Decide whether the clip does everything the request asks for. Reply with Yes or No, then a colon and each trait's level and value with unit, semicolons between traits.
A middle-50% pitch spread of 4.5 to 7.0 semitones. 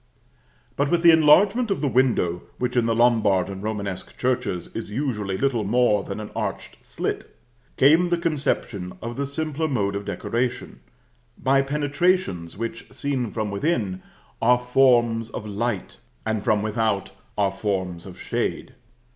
Yes: wide, 5.5 semitones